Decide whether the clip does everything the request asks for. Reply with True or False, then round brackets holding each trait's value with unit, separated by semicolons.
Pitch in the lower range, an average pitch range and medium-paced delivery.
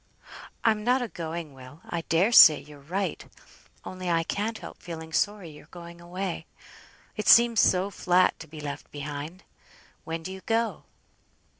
False (175 Hz; 4.0 semitones; 160 wpm)